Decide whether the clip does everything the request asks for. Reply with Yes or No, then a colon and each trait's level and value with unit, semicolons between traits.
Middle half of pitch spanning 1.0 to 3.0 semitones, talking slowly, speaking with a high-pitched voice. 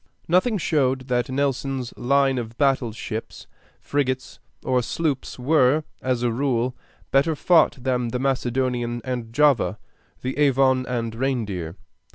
No: narrow, 2.4 semitones; slow, 130 wpm; low, 130 Hz